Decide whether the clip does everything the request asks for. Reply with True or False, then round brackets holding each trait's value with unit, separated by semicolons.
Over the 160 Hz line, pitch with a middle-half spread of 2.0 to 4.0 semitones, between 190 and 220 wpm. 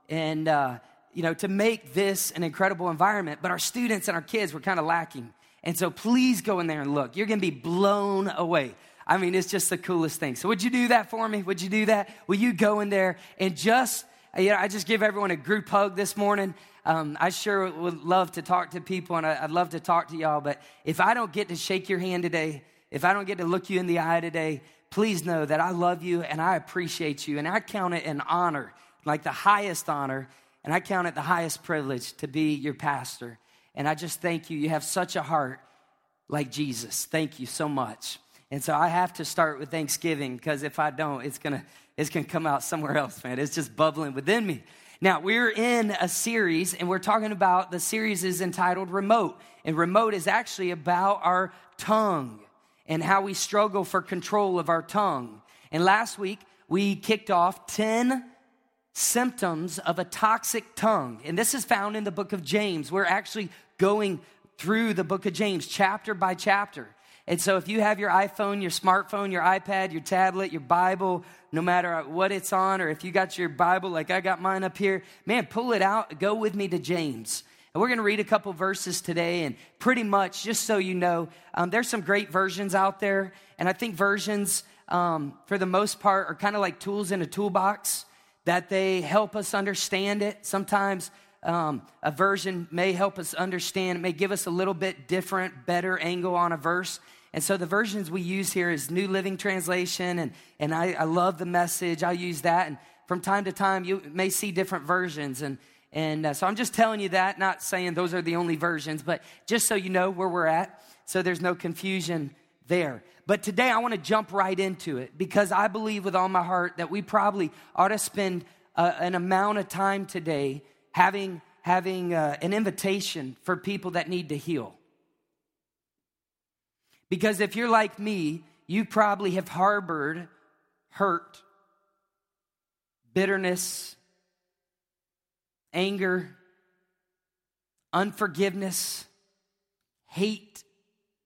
True (185 Hz; 3.0 semitones; 195 wpm)